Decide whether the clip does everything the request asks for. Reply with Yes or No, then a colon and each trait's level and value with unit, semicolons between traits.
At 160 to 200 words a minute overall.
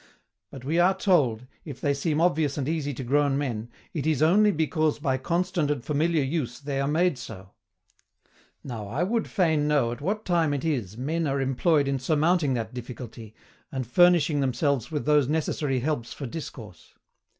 Yes: average, 180 wpm